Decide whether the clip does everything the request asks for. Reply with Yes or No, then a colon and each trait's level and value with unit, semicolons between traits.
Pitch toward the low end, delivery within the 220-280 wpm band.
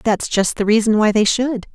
No: high, 215 Hz; fast, 240 wpm